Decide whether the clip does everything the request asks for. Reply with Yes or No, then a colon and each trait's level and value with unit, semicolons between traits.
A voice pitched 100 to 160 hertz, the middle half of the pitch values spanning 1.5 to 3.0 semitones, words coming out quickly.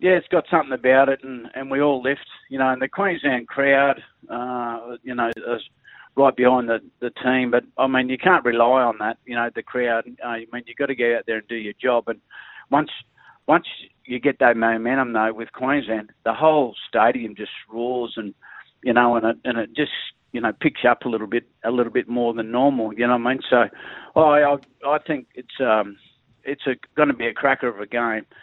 Yes: low, 125 Hz; narrow, 2.6 semitones; fast, 230 wpm